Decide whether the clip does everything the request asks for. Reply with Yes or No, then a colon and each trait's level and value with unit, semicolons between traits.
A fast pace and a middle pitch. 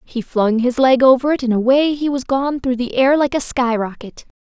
No: fast, 245 wpm; very high, 255 Hz